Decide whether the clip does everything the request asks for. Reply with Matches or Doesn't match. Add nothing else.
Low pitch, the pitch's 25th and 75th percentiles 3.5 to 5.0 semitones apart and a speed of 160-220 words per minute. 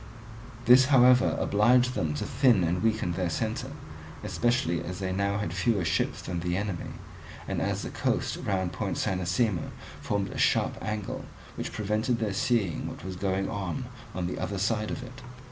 Matches